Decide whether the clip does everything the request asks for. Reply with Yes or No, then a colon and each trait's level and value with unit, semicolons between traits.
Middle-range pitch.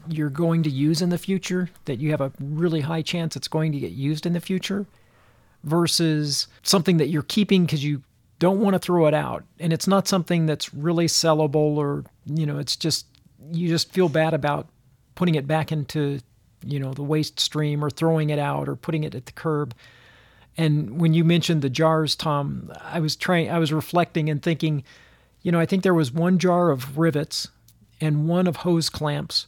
Yes: medium, 155 Hz